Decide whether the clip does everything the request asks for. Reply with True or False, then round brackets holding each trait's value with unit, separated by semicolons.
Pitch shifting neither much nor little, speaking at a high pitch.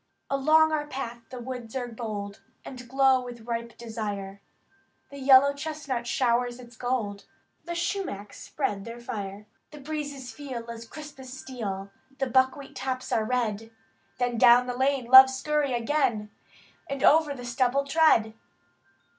True (3.1 semitones; 250 Hz)